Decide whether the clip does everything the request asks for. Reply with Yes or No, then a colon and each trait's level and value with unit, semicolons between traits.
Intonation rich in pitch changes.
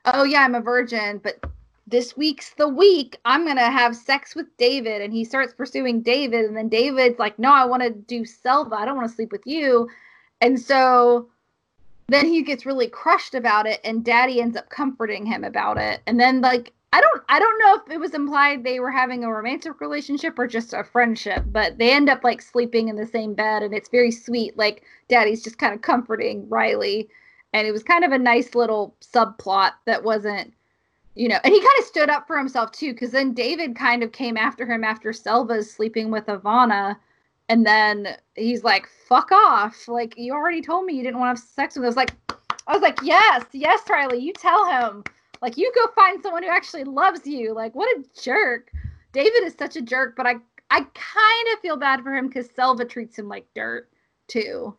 No: average, 4.1 semitones